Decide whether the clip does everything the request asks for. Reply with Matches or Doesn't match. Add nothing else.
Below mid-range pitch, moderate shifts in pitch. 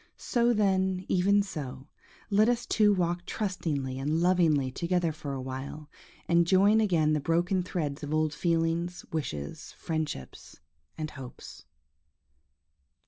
Doesn't match